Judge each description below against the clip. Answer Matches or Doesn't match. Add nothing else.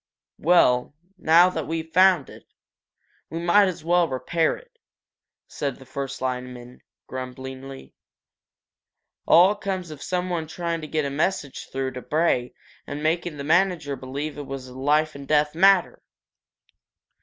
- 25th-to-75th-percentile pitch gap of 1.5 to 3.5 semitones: Doesn't match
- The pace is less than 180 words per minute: Matches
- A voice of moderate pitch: Matches